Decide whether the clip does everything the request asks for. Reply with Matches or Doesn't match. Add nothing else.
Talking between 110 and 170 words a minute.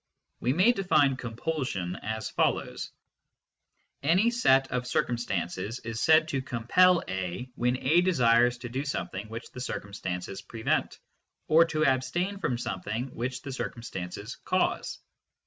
Matches